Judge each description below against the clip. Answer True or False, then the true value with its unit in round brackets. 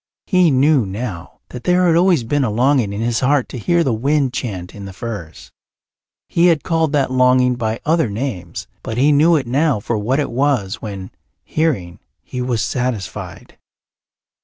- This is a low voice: True (125 Hz)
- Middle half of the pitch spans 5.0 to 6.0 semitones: True (5.3 semitones)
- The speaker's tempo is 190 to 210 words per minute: False (180 wpm)